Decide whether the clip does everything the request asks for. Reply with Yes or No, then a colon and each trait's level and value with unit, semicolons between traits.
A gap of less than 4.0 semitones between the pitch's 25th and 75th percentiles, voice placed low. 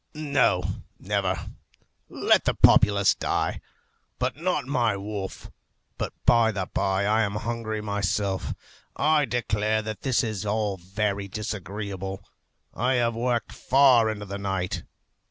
Yes: average, 2.9 semitones; low, 105 Hz